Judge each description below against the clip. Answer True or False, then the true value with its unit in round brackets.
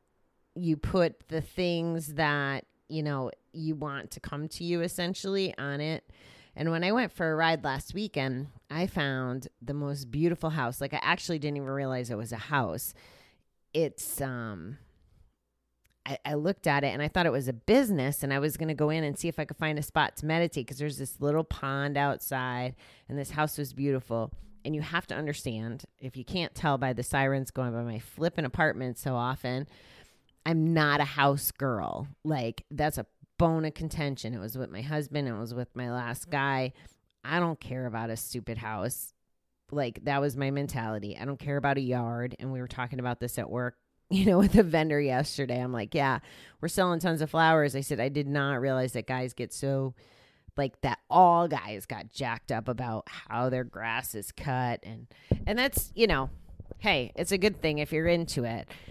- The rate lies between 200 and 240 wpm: True (205 wpm)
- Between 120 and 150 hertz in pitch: True (140 Hz)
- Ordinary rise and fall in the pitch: True (3.9 semitones)